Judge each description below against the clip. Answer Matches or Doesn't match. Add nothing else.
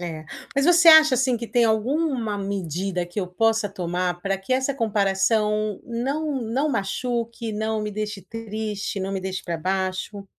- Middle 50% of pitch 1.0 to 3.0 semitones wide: Doesn't match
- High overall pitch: Matches